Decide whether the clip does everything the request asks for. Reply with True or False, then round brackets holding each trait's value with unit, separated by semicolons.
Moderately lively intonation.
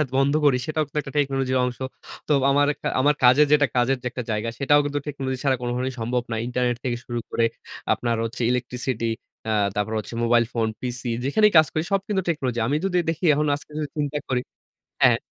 True (3.2 semitones)